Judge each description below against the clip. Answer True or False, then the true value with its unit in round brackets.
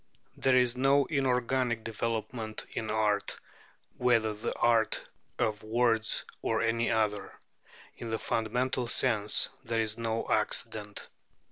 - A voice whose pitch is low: True (115 Hz)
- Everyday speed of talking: False (120 wpm)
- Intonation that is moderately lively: False (2.1 semitones)